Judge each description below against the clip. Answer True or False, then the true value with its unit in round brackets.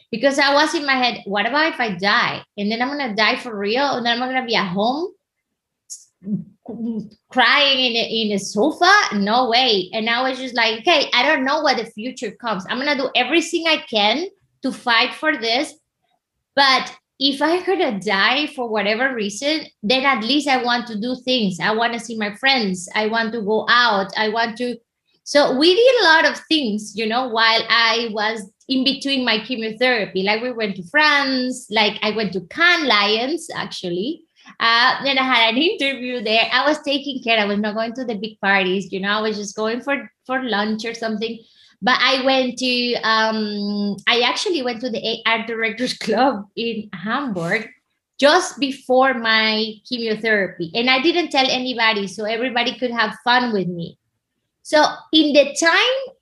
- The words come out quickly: True (195 wpm)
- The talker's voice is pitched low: False (235 Hz)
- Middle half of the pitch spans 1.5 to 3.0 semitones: False (3.7 semitones)